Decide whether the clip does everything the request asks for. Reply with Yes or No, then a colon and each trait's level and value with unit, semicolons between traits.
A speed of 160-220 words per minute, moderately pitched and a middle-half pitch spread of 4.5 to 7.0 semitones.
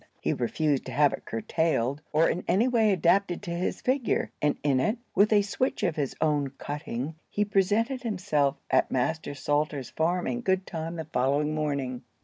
Yes: average, 180 wpm; medium, 160 Hz; wide, 5.5 semitones